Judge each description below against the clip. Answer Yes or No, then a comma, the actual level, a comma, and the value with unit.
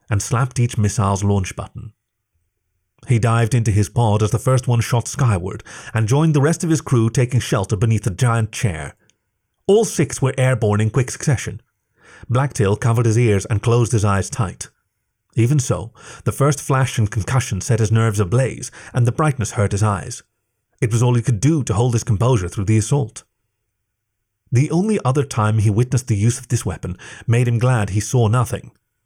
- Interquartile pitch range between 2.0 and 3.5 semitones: Yes, average, 3.1 semitones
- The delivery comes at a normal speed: Yes, average, 190 wpm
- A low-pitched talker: Yes, low, 115 Hz